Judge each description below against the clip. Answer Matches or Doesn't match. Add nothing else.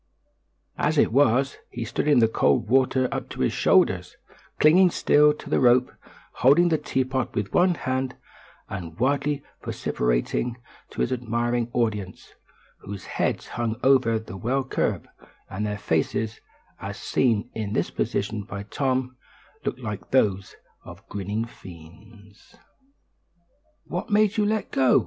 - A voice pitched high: Doesn't match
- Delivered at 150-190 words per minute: Doesn't match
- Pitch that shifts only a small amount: Doesn't match